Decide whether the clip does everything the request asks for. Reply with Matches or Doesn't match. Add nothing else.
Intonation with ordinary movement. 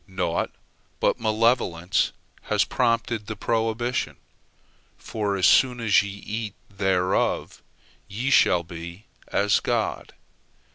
Matches